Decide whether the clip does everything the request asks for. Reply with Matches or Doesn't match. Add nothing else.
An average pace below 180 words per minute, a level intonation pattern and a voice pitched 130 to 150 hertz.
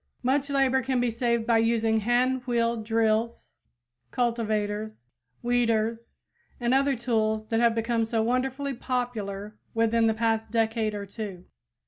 Doesn't match